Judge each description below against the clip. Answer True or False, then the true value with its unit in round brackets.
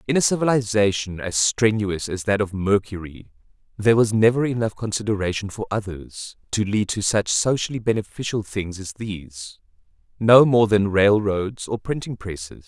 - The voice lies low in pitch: True (105 Hz)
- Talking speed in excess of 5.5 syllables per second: False (5.0 syllables/s)